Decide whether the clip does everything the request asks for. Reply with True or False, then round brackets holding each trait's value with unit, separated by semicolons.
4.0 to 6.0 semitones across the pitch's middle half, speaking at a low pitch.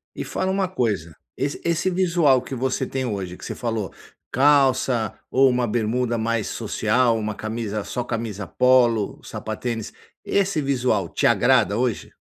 False (3.5 semitones; 120 Hz)